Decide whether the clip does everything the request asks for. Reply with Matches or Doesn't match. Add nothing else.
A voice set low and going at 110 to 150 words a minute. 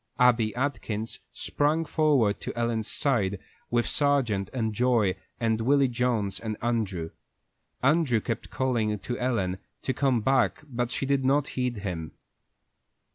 Matches